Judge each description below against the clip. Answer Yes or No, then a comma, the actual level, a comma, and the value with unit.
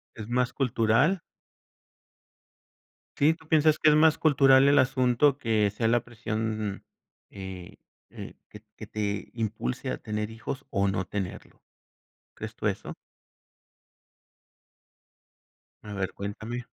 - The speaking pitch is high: No, low, 115 Hz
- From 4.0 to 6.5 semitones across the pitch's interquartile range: Yes, average, 4.7 semitones